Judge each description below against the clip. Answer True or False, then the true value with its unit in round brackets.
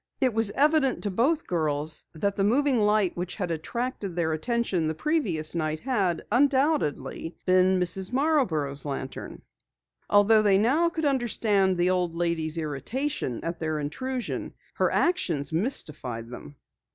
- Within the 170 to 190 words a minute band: False (140 wpm)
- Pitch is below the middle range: False (190 Hz)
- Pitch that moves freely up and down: True (8.0 semitones)